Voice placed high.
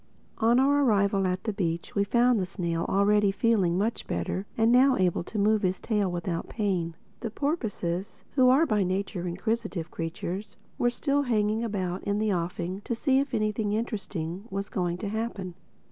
Yes: high, 205 Hz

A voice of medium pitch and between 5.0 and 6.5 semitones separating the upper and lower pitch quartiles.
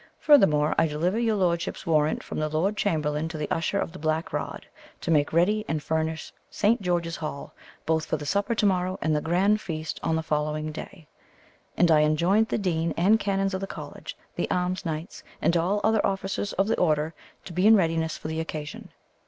No: medium, 165 Hz; average, 3.8 semitones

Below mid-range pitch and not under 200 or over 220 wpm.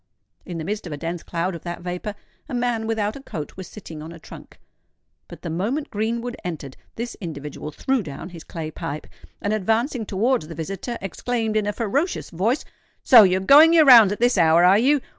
No: high, 205 Hz; fast, 205 wpm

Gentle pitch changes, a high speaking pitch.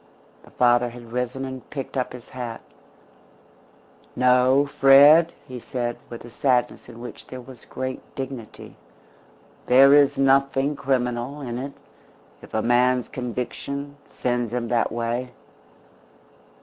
No: narrow, 1.9 semitones; low, 125 Hz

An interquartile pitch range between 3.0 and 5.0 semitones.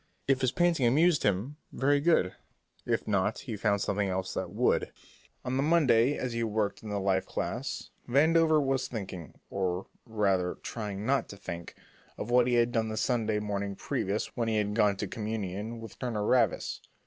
Yes: average, 4.2 semitones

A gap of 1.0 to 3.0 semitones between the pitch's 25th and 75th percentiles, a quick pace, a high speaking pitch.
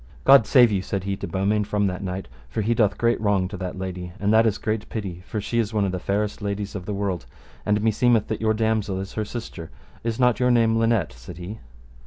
No: average, 2.7 semitones; fast, 245 wpm; low, 105 Hz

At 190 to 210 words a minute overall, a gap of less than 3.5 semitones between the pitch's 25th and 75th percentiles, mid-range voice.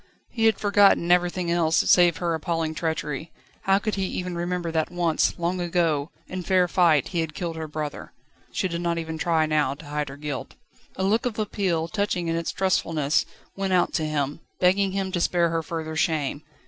Yes: average, 200 wpm; narrow, 2.5 semitones; medium, 170 Hz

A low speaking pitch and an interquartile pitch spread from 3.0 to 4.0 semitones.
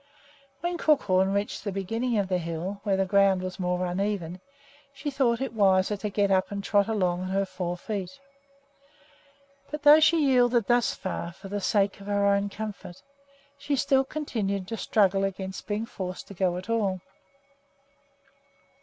No: high, 200 Hz; average, 3.3 semitones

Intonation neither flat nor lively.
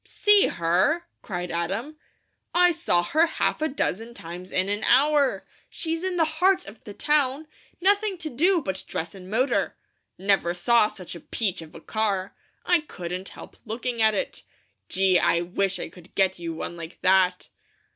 No: wide, 9.0 semitones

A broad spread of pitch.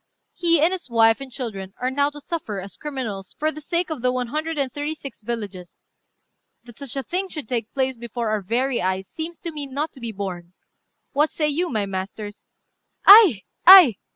Yes: wide, 6.1 semitones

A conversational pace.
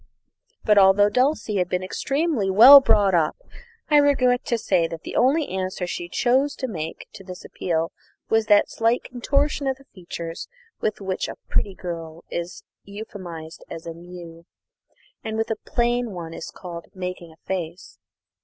Yes: average, 165 wpm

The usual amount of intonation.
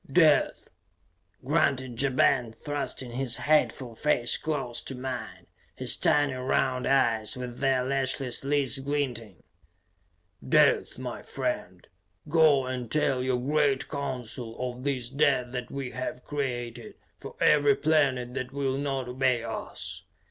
No: narrow, 2.3 semitones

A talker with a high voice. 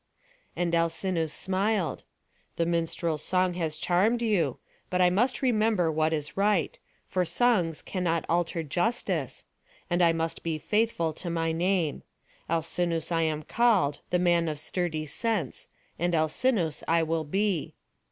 No: medium, 170 Hz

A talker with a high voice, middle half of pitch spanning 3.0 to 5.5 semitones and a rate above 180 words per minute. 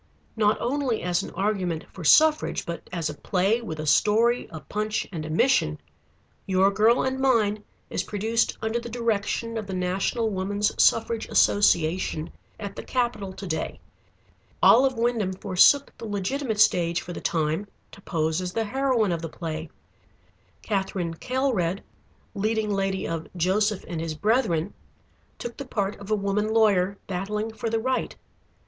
No: high, 205 Hz; average, 4.0 semitones; average, 160 wpm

